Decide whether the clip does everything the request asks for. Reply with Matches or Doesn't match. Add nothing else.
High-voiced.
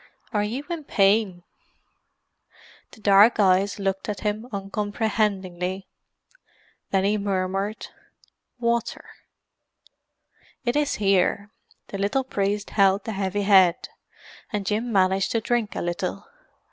Matches